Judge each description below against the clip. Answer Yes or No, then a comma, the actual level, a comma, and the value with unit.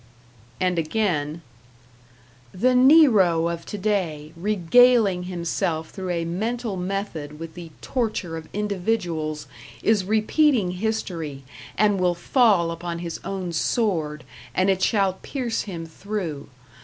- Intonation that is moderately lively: Yes, average, 4.3 semitones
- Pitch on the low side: No, medium, 185 Hz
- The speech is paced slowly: Yes, slow, 120 wpm